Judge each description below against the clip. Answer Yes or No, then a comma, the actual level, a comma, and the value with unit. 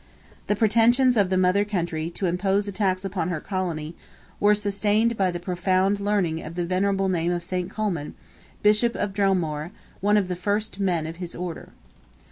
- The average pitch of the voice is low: No, high, 190 Hz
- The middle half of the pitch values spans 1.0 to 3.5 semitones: Yes, average, 2.8 semitones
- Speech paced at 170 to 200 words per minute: Yes, average, 175 wpm